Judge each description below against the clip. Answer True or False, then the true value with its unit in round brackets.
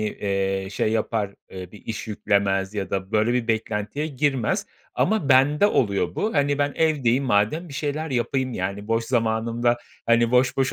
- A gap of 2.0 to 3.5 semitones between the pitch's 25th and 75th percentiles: False (4.7 semitones)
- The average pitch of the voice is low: True (115 Hz)